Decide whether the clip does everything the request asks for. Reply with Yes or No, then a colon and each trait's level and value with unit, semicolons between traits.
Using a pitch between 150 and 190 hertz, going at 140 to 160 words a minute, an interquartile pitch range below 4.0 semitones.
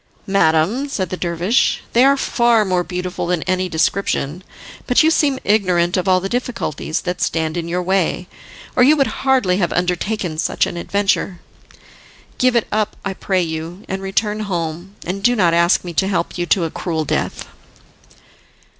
No: medium, 185 Hz; average, 175 wpm; average, 3.6 semitones